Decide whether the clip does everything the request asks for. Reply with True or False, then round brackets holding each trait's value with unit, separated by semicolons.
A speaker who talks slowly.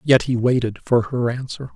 False (205 wpm)